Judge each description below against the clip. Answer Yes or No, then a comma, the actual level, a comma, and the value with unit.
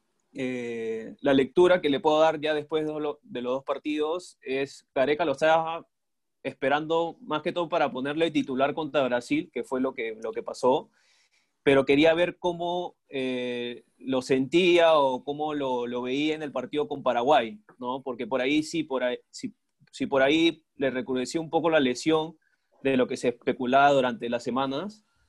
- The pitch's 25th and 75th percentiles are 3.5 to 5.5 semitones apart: Yes, average, 3.8 semitones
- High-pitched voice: No, medium, 145 Hz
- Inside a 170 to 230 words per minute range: Yes, average, 175 wpm